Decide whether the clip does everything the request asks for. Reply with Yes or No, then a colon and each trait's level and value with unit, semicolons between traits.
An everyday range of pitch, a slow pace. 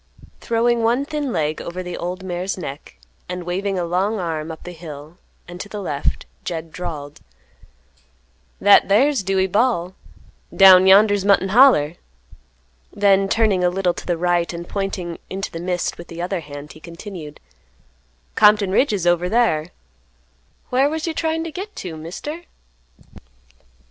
No: average, 3.5 semitones; average, 155 wpm